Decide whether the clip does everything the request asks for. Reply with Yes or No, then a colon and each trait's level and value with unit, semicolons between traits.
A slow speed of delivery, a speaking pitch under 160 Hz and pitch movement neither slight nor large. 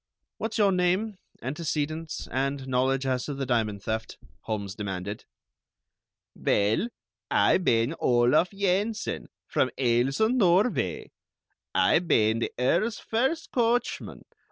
No: slow, 110 wpm; low, 135 Hz; wide, 8.9 semitones